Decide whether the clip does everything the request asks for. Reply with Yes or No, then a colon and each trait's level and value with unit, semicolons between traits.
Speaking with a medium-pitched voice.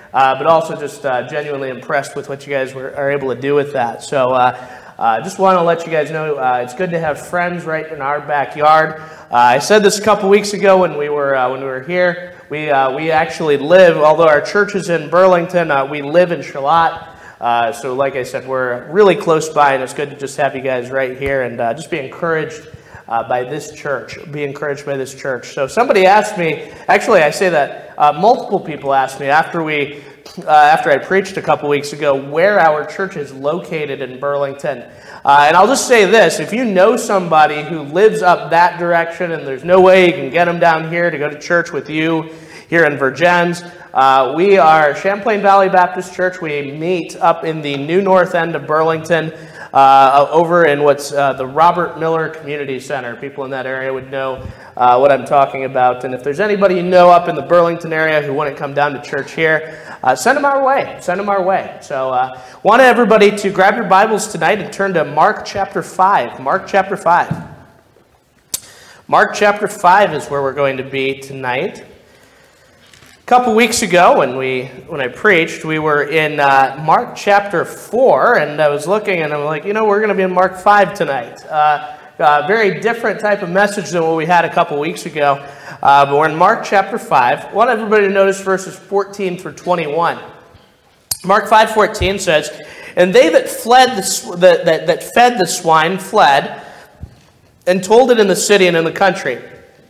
Yes: medium, 160 Hz